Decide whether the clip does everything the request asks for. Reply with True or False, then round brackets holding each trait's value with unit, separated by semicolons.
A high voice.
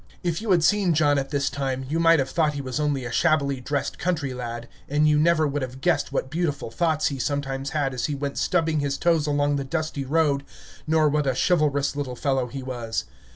False (145 Hz)